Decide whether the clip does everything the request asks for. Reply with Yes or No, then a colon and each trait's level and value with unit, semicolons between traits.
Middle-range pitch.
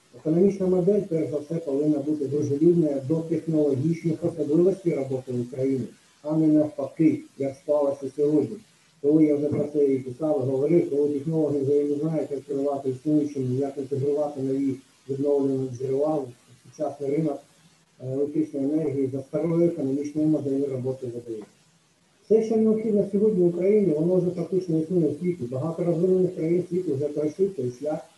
Yes: medium, 150 Hz